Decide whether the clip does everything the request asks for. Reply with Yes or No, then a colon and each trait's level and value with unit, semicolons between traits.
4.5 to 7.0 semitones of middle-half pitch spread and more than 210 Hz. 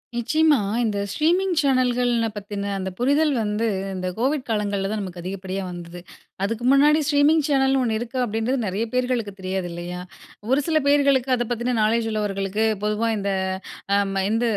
Yes: average, 5.1 semitones; high, 230 Hz